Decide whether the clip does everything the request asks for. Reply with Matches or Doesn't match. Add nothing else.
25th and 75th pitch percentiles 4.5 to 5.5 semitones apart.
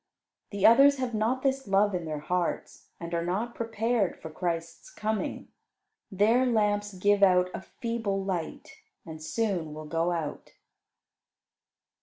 Matches